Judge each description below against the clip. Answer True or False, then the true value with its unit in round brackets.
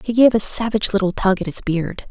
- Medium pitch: False (200 Hz)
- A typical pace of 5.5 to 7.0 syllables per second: True (6.2 syllables/s)